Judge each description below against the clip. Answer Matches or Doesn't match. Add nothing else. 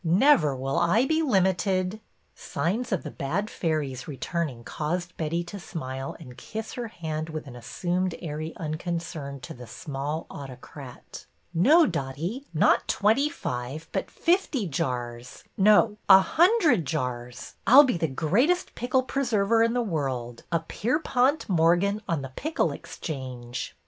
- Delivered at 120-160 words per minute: Matches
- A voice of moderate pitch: Matches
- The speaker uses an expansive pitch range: Matches